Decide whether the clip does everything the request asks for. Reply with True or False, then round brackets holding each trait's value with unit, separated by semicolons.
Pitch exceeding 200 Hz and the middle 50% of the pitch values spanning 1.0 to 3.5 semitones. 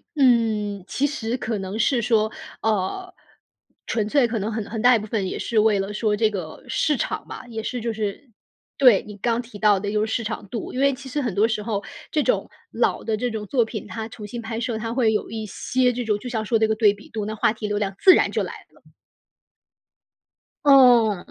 True (220 Hz; 2.5 semitones)